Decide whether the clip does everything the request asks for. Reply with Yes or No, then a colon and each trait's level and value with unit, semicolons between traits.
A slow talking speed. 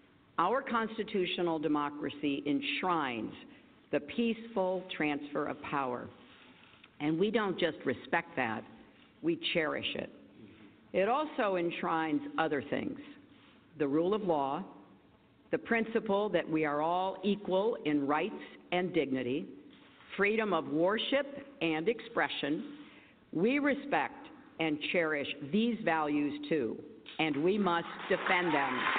Yes: slow, 115 wpm